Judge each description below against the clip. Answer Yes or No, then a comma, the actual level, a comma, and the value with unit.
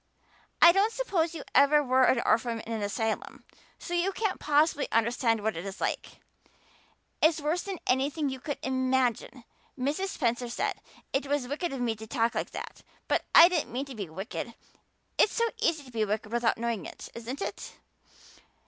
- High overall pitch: Yes, very high, 260 Hz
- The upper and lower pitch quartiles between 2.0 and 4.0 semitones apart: No, average, 5.1 semitones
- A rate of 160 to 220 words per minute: Yes, average, 185 wpm